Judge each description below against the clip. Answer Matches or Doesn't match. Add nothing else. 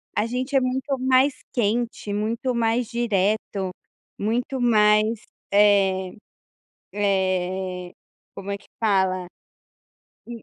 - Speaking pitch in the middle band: Doesn't match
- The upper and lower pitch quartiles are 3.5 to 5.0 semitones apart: Matches